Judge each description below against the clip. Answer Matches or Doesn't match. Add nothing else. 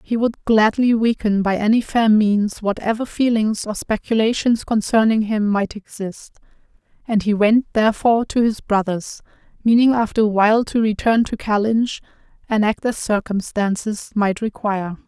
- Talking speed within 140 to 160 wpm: Matches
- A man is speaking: Doesn't match